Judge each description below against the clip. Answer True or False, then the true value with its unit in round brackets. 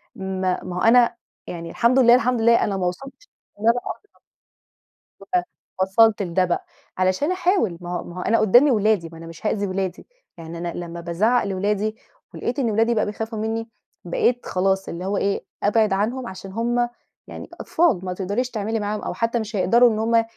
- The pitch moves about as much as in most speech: True (4.0 semitones)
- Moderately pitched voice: False (210 Hz)